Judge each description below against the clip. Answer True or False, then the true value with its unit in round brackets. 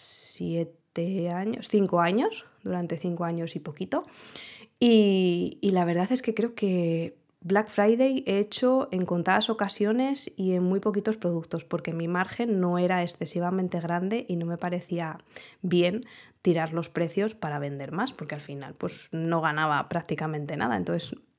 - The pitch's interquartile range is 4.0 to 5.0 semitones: False (3.6 semitones)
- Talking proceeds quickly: False (155 wpm)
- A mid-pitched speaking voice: True (180 Hz)